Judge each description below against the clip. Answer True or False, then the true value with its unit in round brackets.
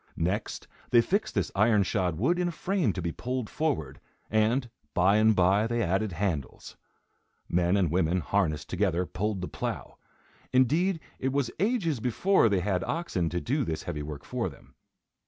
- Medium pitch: False (105 Hz)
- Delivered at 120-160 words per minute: False (175 wpm)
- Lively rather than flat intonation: True (6.4 semitones)